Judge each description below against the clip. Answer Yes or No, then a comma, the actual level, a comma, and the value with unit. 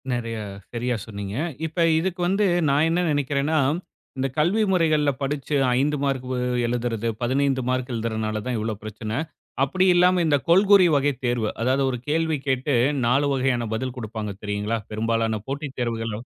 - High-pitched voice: No, low, 130 Hz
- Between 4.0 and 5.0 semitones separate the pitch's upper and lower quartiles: Yes, average, 4.5 semitones